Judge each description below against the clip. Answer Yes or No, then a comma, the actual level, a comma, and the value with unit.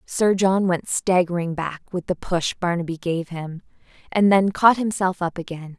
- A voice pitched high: No, medium, 180 Hz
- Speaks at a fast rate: No, average, 175 wpm